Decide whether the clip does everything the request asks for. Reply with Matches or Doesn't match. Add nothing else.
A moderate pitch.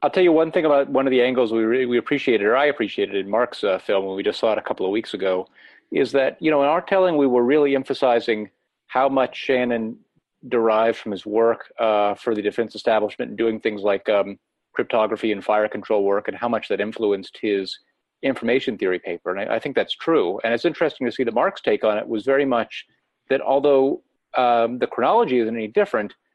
Doesn't match